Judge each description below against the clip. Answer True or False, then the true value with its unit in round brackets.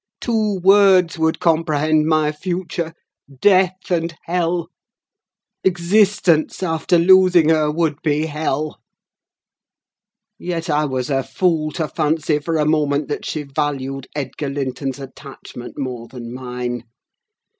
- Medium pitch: True (155 Hz)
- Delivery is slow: True (115 wpm)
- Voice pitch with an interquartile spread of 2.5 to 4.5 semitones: True (3.4 semitones)